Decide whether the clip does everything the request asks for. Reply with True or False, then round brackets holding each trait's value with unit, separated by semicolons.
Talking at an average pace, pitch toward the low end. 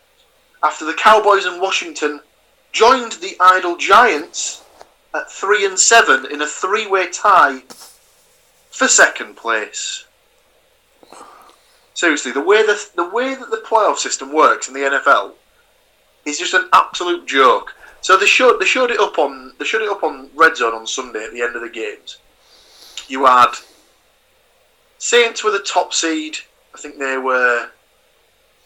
False (155 wpm; 215 Hz)